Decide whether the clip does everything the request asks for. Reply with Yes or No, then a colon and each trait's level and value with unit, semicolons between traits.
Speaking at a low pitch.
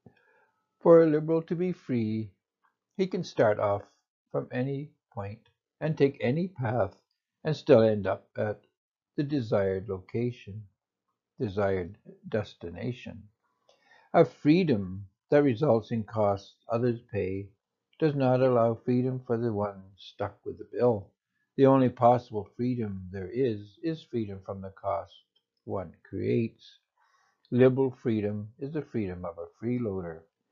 Yes: low, 115 Hz